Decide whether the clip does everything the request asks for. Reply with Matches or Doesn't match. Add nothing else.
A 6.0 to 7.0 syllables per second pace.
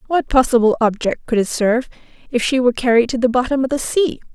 Matches